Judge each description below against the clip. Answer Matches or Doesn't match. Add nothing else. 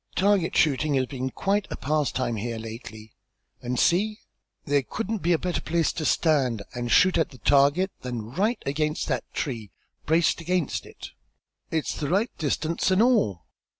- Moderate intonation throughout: Doesn't match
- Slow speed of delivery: Doesn't match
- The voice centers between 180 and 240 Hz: Doesn't match